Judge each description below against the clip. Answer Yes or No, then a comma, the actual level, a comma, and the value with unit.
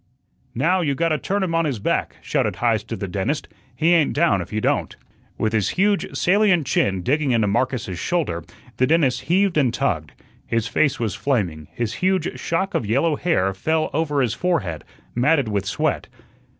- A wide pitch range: Yes, wide, 7.6 semitones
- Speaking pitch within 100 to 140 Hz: Yes, low, 135 Hz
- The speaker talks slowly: No, average, 180 wpm